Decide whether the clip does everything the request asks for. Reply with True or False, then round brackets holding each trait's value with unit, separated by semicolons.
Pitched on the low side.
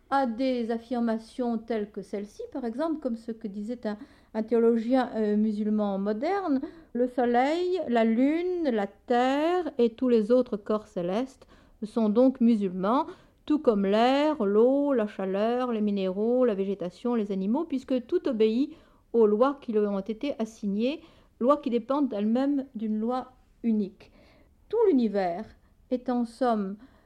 False (235 Hz)